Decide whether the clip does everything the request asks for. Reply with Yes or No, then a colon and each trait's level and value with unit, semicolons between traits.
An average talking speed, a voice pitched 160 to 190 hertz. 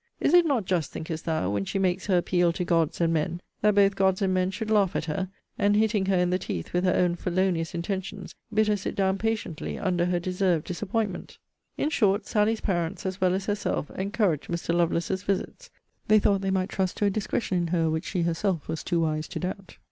No: fast, 225 wpm; medium, 185 Hz